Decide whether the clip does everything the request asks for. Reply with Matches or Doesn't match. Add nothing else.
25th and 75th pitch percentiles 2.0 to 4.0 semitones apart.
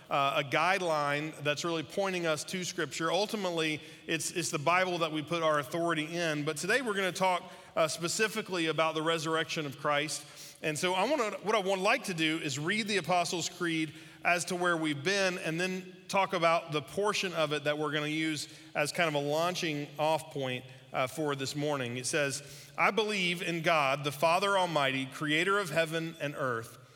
Matches